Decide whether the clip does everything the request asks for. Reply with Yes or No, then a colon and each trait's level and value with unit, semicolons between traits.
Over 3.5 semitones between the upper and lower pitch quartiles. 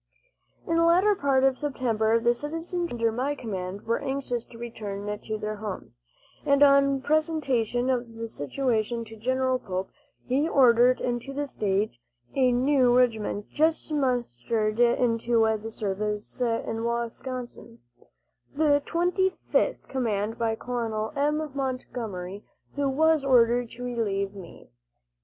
Yes: average, 3.9 semitones